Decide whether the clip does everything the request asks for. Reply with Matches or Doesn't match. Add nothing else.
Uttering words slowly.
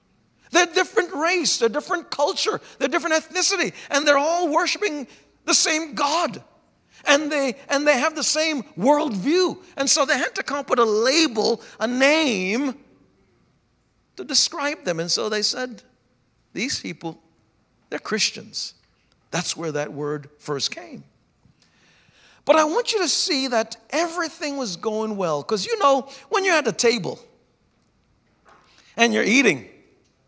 Doesn't match